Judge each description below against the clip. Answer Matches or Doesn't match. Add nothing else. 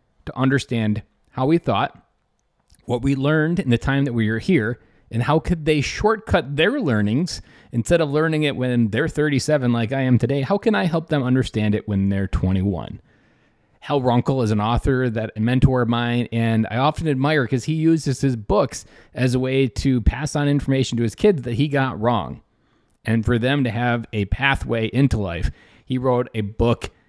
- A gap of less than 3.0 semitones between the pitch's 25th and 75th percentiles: Doesn't match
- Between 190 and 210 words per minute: Matches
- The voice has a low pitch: Matches